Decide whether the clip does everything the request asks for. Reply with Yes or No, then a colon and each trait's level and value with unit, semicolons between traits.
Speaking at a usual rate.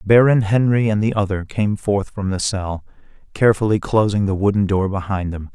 Yes: average, 185 wpm